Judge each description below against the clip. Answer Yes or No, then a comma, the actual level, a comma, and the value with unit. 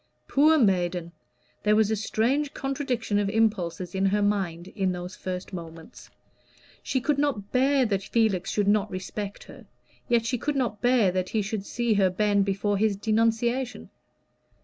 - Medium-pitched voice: No, high, 210 Hz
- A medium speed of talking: Yes, average, 165 wpm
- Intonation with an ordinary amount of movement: Yes, average, 3.8 semitones